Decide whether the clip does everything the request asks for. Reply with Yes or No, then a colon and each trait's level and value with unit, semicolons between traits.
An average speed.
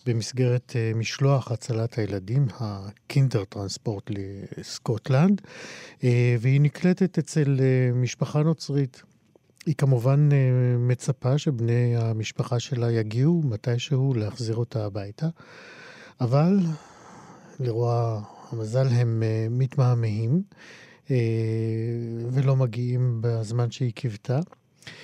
No: slow, 80 wpm